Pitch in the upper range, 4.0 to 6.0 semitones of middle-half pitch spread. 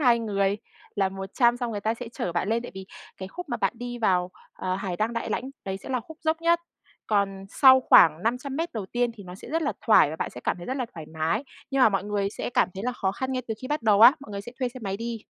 Yes: high, 225 Hz; average, 4.5 semitones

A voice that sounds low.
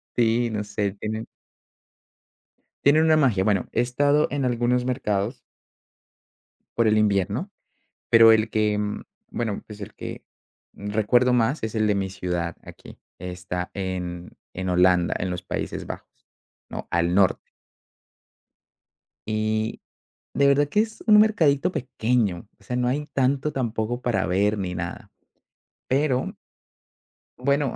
Yes: low, 110 Hz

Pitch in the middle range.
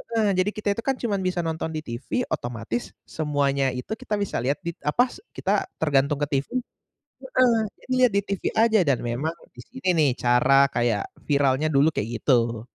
Yes: medium, 150 Hz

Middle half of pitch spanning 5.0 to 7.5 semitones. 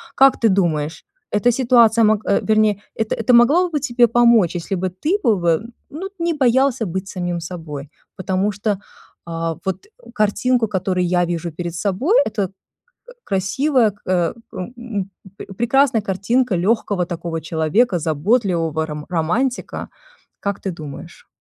Yes: wide, 5.5 semitones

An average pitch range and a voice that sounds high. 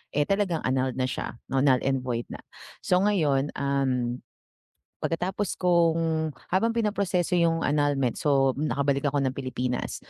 No: average, 4.6 semitones; medium, 145 Hz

